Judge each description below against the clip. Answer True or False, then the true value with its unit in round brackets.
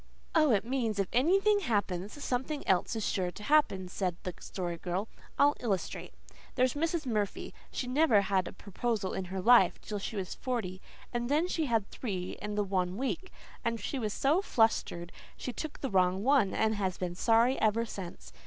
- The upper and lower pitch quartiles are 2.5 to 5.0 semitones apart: False (5.6 semitones)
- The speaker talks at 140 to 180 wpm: False (190 wpm)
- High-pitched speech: True (220 Hz)